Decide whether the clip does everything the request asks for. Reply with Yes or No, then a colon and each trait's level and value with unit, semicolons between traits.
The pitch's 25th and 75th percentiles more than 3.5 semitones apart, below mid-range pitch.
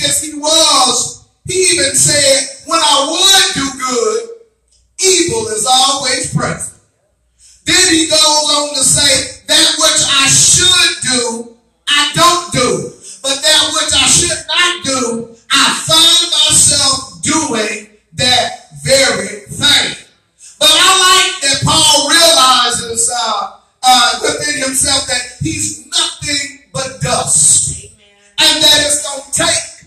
No: average, 4.3 semitones; very high, 290 Hz